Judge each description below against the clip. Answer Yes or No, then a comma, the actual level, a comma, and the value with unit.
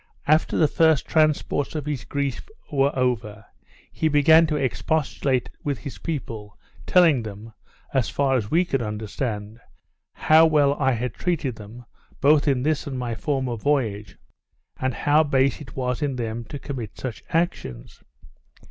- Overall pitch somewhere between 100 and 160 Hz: Yes, low, 135 Hz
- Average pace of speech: Yes, average, 155 wpm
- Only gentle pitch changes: No, average, 4.4 semitones